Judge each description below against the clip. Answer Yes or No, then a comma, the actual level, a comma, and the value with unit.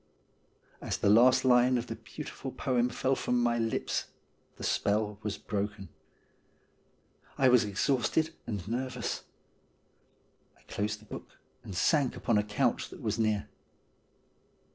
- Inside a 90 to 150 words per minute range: Yes, slow, 135 wpm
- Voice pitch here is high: No, low, 115 Hz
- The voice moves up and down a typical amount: Yes, average, 3.4 semitones